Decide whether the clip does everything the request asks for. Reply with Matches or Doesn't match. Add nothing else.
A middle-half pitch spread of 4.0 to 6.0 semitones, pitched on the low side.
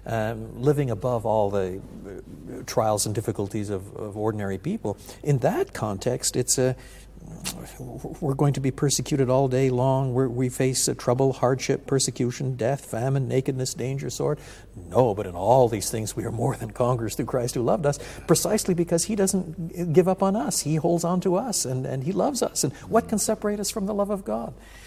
Matches